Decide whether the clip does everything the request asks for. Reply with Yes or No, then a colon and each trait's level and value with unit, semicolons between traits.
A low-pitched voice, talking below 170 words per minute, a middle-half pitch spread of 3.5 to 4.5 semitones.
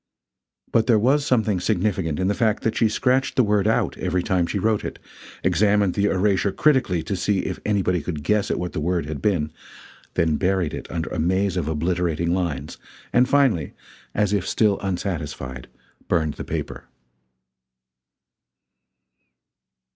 Yes: very low, 95 Hz; average, 160 wpm; average, 3.8 semitones